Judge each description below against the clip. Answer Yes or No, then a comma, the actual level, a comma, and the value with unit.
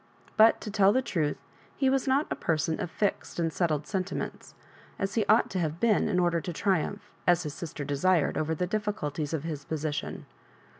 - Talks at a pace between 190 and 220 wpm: Yes, average, 195 wpm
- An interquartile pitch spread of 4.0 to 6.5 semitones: Yes, average, 4.9 semitones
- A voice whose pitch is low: No, medium, 175 Hz